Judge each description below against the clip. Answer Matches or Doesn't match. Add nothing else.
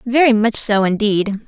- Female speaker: Matches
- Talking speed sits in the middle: Matches